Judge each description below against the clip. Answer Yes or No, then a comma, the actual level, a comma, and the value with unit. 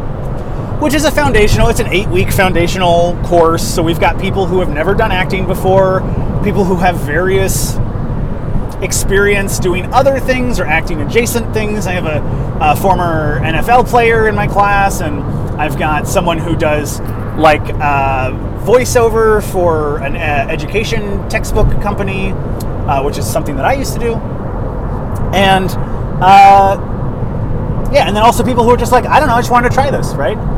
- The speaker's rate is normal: Yes, average, 170 wpm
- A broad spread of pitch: Yes, wide, 8.4 semitones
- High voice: No, low, 135 Hz